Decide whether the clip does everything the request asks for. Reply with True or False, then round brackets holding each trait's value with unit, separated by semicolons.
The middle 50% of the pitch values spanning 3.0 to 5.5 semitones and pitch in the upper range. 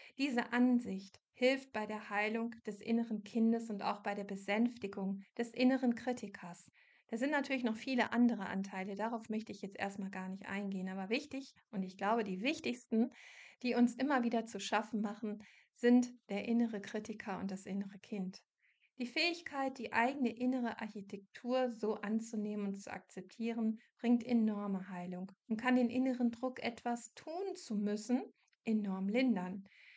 True (3.3 semitones; 225 Hz)